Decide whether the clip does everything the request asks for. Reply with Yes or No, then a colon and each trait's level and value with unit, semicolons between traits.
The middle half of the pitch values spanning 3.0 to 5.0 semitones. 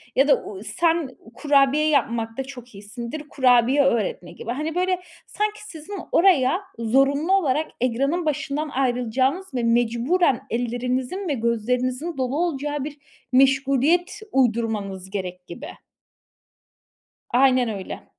Yes: average, 4.5 semitones